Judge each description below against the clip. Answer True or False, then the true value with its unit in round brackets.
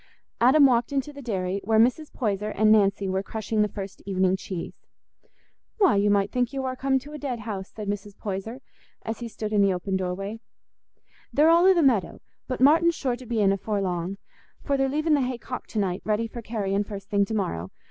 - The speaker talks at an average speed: False (220 wpm)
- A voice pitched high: True (215 Hz)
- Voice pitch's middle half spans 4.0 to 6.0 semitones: True (4.7 semitones)